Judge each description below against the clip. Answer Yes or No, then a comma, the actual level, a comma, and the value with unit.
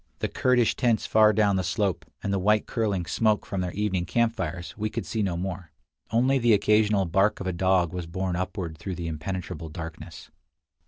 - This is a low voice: Yes, very low, 95 Hz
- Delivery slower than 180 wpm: No, average, 200 wpm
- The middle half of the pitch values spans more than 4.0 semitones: No, average, 3.5 semitones